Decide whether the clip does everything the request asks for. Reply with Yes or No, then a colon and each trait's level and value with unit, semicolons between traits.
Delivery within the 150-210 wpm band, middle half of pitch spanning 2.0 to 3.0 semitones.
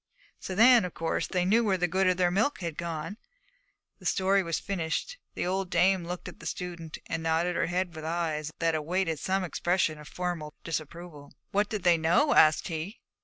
Yes: average, 200 wpm; average, 2.7 semitones